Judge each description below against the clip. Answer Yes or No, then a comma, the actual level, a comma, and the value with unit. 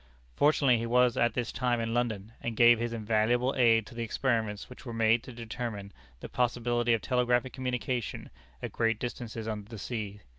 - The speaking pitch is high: No, low, 120 Hz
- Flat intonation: Yes, narrow, 1.6 semitones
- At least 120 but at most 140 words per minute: No, average, 185 wpm